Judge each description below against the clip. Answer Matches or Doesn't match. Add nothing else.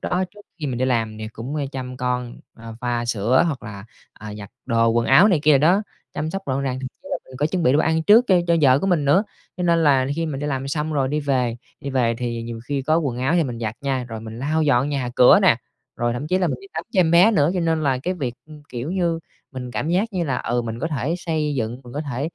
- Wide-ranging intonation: Doesn't match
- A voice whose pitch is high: Doesn't match